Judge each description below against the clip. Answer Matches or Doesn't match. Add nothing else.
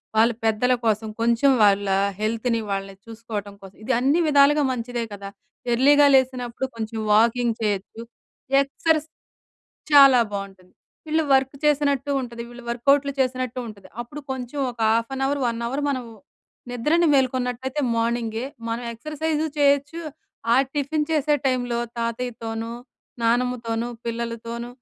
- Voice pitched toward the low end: Doesn't match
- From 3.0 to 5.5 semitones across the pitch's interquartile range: Matches